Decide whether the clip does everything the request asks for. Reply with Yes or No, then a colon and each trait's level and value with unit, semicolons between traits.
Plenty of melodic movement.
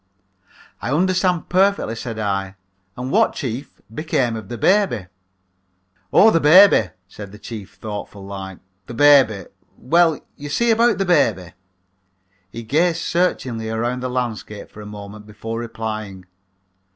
Yes: wide, 7.3 semitones